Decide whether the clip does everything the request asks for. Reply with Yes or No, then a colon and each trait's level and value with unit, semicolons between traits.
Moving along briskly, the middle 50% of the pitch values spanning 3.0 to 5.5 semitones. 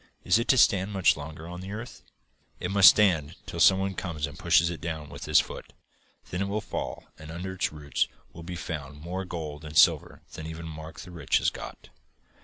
Yes: fast, 215 wpm; average, 3.4 semitones